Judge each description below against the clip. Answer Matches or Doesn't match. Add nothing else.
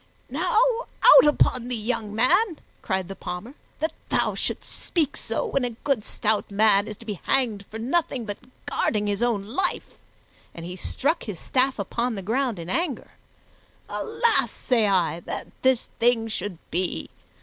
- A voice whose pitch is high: Matches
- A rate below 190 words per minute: Matches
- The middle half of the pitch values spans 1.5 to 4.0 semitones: Doesn't match